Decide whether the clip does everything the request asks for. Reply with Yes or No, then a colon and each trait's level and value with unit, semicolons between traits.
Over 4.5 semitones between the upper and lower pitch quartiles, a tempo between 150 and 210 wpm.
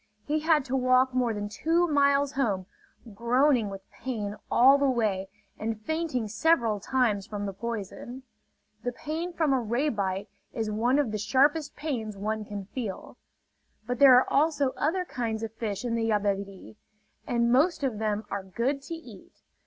Yes: average, 4.9 semitones; average, 170 wpm